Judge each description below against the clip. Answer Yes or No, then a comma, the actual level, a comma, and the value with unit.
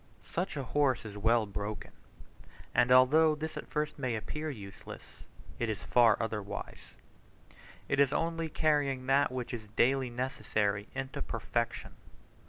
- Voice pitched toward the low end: Yes, low, 130 Hz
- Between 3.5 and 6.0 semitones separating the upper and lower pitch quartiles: Yes, average, 4.7 semitones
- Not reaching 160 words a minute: Yes, average, 140 wpm